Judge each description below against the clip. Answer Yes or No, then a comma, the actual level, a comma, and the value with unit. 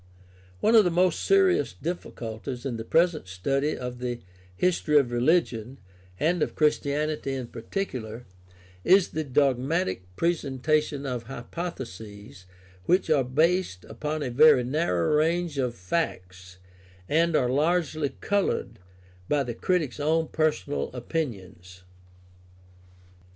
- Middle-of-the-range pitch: Yes, medium, 145 Hz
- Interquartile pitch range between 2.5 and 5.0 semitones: No, wide, 5.4 semitones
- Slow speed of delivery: Yes, slow, 120 wpm